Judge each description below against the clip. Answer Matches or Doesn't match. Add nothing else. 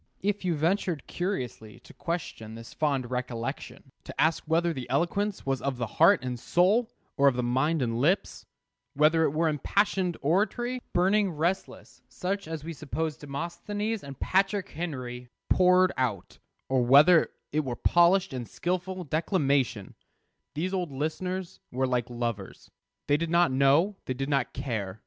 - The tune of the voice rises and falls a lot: Matches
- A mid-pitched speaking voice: Matches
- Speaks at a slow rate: Doesn't match